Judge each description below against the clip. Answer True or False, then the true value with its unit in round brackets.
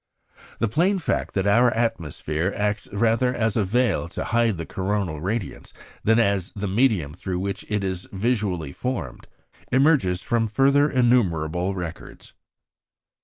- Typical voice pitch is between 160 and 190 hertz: False (105 Hz)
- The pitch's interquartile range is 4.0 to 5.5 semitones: True (4.4 semitones)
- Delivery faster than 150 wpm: False (140 wpm)